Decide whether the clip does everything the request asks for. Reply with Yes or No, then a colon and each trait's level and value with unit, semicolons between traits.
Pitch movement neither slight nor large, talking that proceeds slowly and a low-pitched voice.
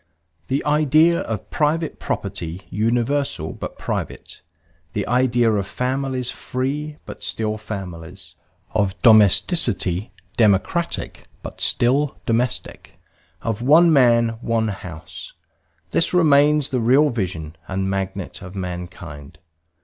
No: wide, 6.3 semitones; slow, 110 wpm; low, 115 Hz